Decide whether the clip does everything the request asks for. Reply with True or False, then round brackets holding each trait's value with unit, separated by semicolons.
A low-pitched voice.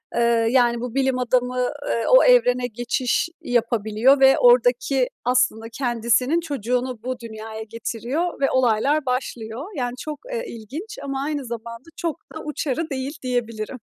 False (250 Hz)